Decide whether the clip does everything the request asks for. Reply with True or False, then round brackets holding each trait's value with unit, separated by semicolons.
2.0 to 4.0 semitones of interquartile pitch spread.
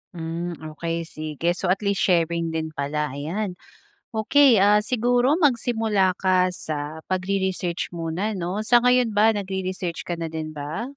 False (4.6 semitones)